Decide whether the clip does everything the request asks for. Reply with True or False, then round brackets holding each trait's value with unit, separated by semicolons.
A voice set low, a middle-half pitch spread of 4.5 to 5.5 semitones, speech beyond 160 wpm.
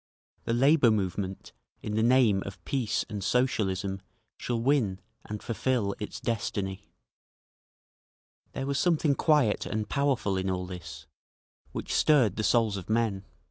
False (110 Hz; 4.8 semitones; 140 wpm)